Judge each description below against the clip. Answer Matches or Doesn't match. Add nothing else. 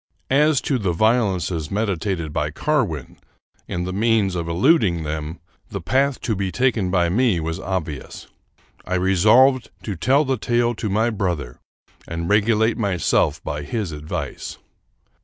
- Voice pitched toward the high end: Doesn't match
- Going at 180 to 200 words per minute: Doesn't match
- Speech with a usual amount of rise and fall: Doesn't match